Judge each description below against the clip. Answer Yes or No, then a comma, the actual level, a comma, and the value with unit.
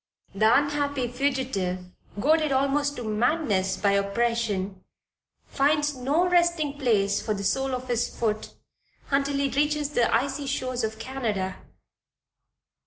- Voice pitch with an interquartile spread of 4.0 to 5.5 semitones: Yes, average, 4.9 semitones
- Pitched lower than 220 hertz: No, very high, 255 Hz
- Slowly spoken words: Yes, slow, 125 wpm